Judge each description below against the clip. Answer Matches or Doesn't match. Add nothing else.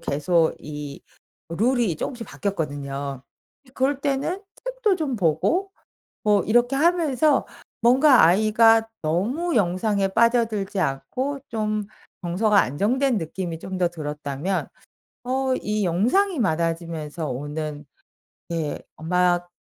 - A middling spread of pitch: Doesn't match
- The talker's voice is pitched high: Matches